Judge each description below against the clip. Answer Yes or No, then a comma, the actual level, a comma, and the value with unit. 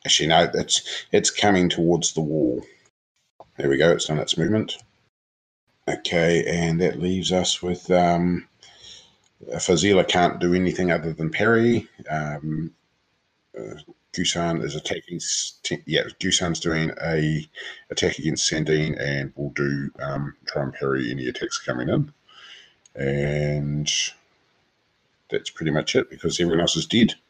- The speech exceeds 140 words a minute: No, slow, 135 wpm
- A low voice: Yes, very low, 80 Hz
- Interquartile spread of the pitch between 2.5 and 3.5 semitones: Yes, average, 3.1 semitones